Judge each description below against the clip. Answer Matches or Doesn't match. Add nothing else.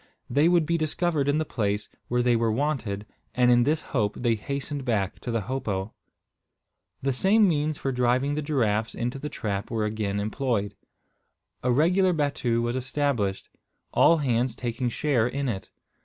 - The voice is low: Matches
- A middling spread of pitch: Matches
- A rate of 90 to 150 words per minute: Doesn't match